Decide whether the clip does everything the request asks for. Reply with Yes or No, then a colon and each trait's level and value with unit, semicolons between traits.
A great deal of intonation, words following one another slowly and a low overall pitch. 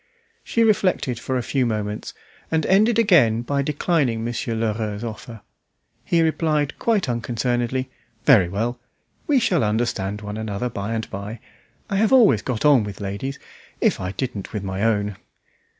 No: wide, 5.9 semitones; average, 155 wpm; low, 120 Hz